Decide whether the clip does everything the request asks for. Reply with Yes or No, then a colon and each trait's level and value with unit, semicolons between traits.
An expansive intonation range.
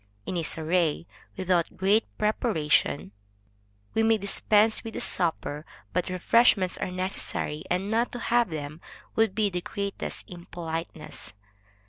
No: average, 4.4 semitones